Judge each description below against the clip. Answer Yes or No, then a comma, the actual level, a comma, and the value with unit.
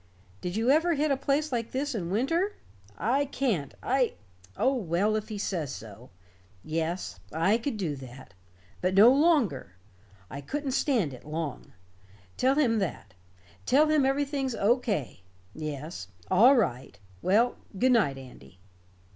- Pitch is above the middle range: Yes, high, 220 Hz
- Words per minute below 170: Yes, average, 145 wpm